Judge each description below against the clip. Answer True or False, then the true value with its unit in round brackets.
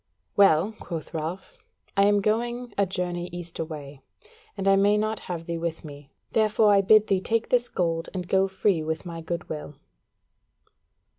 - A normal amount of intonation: True (3.8 semitones)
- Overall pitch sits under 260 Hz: True (185 Hz)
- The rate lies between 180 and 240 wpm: False (165 wpm)